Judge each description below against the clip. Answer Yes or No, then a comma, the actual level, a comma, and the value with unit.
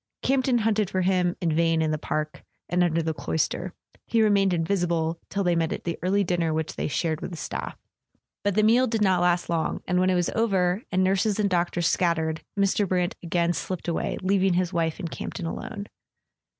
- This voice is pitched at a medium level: Yes, medium, 180 Hz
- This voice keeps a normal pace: No, fast, 210 wpm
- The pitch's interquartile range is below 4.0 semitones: Yes, average, 2.9 semitones